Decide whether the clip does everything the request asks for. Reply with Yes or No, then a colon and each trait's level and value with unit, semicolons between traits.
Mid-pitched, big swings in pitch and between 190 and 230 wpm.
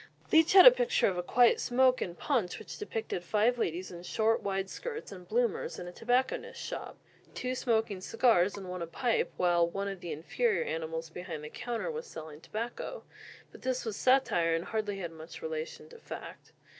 No: high, 215 Hz; wide, 6.5 semitones; average, 195 wpm